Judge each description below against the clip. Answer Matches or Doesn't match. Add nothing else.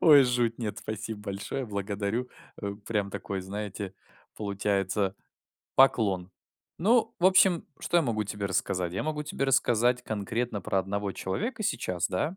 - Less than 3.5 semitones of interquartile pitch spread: Doesn't match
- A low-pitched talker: Matches